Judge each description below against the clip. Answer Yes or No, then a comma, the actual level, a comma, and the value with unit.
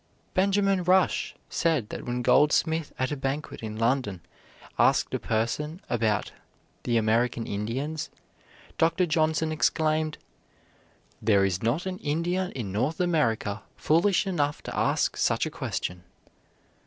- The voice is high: No, medium, 145 Hz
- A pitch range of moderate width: No, wide, 6.3 semitones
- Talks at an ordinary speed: No, slow, 130 wpm